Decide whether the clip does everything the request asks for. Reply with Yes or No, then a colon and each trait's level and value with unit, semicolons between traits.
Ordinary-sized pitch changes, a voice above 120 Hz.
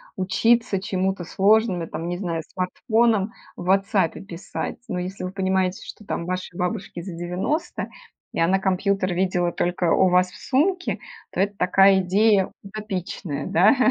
No: narrow, 2.2 semitones; high, 190 Hz